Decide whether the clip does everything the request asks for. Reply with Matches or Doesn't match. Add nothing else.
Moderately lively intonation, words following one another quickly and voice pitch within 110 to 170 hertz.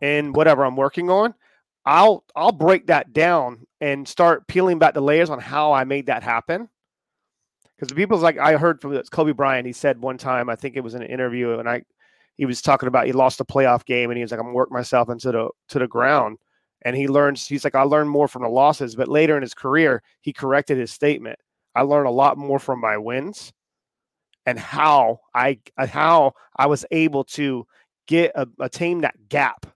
Matches